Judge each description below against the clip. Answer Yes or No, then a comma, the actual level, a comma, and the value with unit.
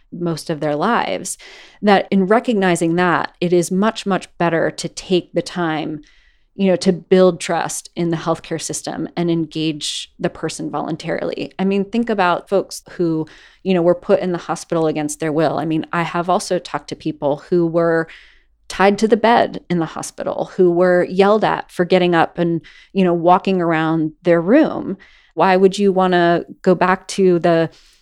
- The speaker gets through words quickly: No, average, 185 wpm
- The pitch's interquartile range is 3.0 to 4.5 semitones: No, narrow, 2.4 semitones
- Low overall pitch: No, medium, 175 Hz